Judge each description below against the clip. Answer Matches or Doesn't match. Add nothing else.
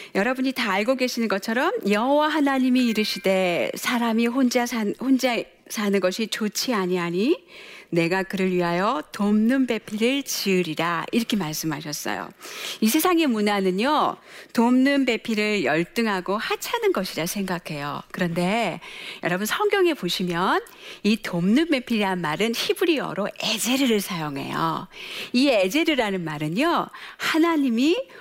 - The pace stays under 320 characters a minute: Matches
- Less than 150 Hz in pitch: Doesn't match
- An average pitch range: Doesn't match